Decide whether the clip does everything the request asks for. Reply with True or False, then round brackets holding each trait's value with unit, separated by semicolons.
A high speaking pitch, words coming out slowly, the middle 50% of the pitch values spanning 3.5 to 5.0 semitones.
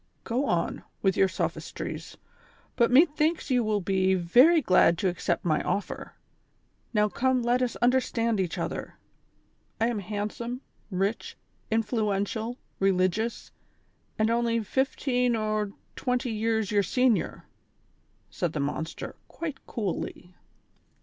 True (220 Hz; 120 wpm; 4.1 semitones)